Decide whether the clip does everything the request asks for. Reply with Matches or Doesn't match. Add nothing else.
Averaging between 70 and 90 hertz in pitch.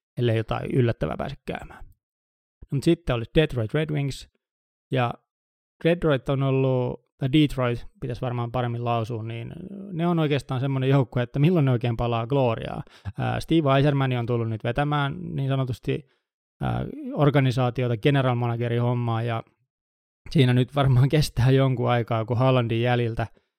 Doesn't match